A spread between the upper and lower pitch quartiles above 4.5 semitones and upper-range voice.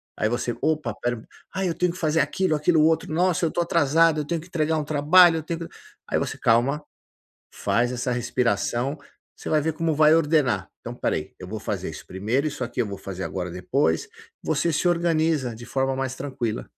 No: average, 5.2 semitones; medium, 145 Hz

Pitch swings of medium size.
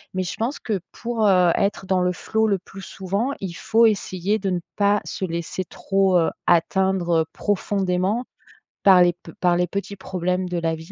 No: narrow, 2.2 semitones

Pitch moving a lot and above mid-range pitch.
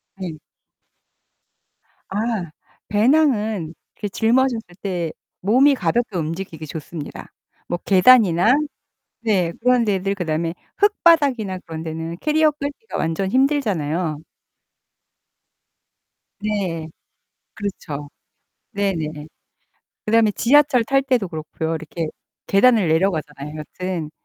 Yes: wide, 6.7 semitones; high, 195 Hz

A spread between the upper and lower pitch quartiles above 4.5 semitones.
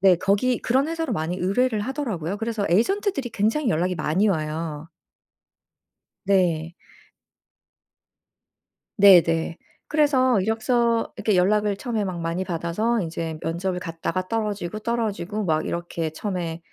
Yes: average, 5.2 semitones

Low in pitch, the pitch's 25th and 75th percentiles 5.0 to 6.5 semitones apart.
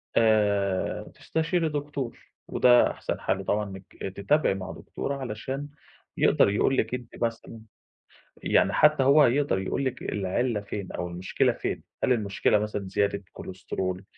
Yes: low, 110 Hz; average, 5.3 semitones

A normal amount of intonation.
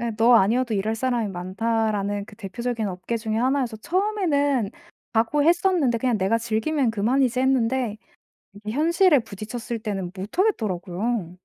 Yes: average, 3.9 semitones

